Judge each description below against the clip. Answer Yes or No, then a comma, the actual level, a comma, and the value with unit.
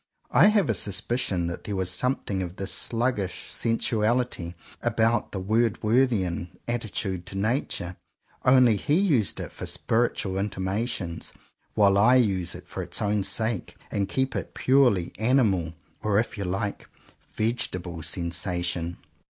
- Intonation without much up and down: No, average, 4.4 semitones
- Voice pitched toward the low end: Yes, low, 105 Hz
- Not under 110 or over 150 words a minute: Yes, average, 140 wpm